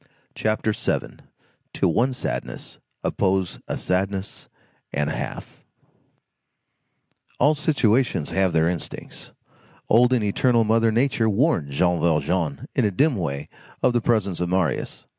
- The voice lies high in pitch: No, low, 100 Hz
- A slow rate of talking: Yes, slow, 125 wpm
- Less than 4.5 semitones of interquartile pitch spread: No, average, 5.3 semitones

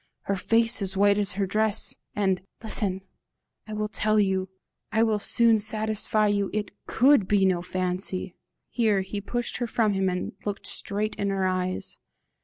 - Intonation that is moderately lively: No, narrow, 2.2 semitones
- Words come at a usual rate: Yes, average, 170 wpm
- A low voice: No, high, 205 Hz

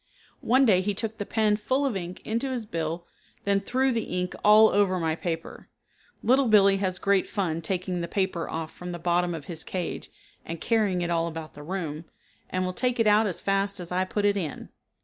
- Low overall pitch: No, high, 190 Hz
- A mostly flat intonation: No, average, 3.6 semitones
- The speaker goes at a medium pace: No, fast, 215 wpm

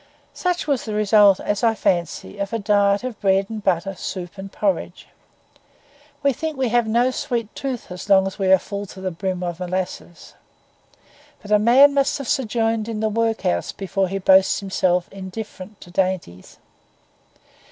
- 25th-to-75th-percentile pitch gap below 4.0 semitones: Yes, average, 3.3 semitones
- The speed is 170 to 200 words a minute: Yes, average, 175 wpm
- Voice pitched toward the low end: No, high, 200 Hz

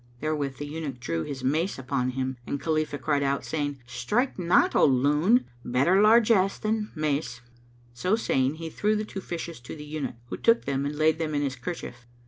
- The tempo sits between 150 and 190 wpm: No, fast, 205 wpm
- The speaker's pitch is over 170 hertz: No, medium, 150 Hz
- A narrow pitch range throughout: No, average, 4.8 semitones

